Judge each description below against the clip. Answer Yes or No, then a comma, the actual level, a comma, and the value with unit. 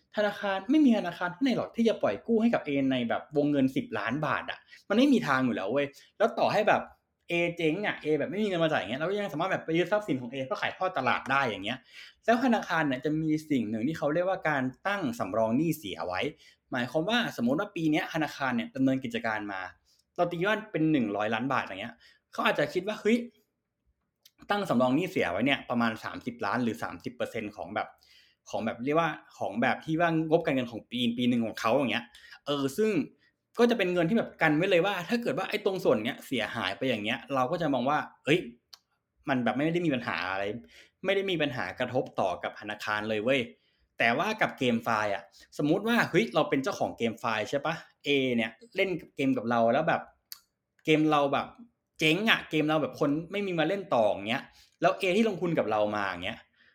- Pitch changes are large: Yes, wide, 7.7 semitones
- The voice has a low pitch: No, medium, 155 Hz